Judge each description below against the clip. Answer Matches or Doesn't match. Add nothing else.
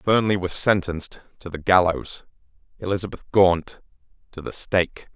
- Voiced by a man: Matches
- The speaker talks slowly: Matches